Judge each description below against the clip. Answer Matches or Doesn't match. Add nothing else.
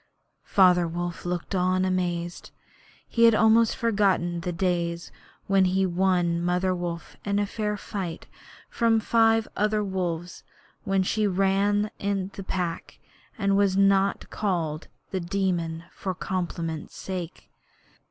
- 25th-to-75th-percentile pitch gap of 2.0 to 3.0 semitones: Matches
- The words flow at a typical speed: Doesn't match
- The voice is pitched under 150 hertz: Doesn't match